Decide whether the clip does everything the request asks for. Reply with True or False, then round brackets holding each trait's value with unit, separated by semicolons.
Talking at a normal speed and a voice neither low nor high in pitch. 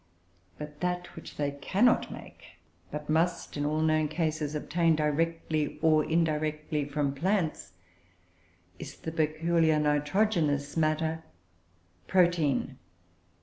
False (105 wpm; 155 Hz)